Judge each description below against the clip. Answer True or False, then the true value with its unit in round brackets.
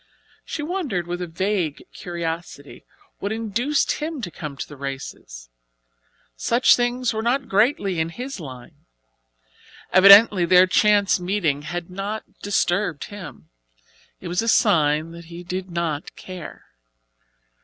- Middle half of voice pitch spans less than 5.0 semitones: True (4.5 semitones)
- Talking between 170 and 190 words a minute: False (135 wpm)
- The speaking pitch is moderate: True (180 Hz)